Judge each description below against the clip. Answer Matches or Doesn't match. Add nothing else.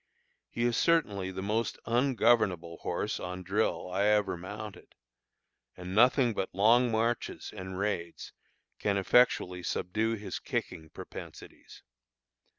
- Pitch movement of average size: Matches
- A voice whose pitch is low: Matches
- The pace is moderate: Doesn't match